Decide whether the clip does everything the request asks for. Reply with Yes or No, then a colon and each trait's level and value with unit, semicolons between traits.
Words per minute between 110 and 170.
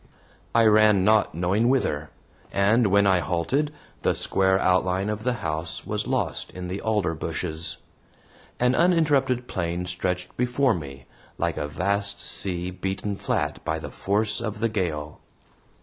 Yes: average, 150 wpm